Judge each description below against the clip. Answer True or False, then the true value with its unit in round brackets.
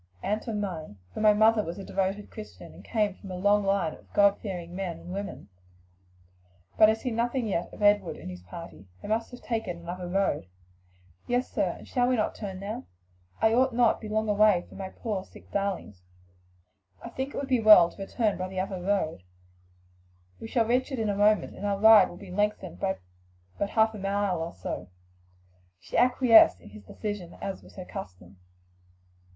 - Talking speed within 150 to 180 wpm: False (200 wpm)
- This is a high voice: True (200 Hz)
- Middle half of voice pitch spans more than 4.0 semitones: False (3.2 semitones)